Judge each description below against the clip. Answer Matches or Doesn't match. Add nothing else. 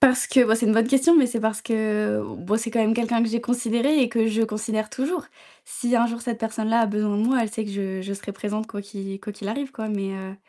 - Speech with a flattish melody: Matches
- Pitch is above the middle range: Matches